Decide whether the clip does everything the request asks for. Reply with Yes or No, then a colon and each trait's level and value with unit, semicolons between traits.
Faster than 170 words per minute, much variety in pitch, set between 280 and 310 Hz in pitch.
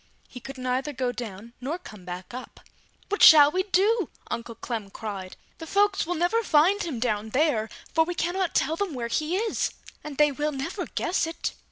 Yes: average, 200 wpm; wide, 6.9 semitones; very high, 295 Hz